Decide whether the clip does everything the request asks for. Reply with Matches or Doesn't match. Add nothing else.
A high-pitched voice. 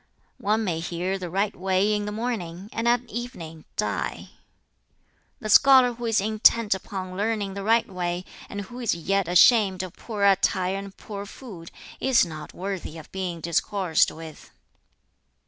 Matches